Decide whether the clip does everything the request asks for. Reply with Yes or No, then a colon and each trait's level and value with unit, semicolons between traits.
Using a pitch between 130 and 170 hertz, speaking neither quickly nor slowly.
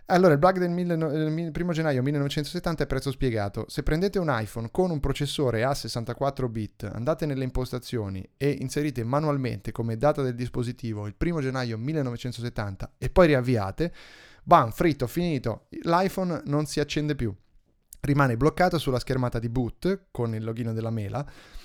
Yes: low, 135 Hz; average, 155 wpm